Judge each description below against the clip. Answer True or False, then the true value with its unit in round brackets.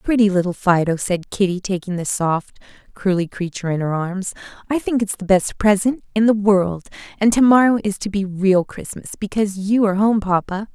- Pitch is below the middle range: False (195 Hz)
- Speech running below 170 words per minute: False (195 wpm)